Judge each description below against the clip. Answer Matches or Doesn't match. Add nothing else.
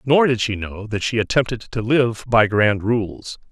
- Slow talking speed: Doesn't match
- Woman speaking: Doesn't match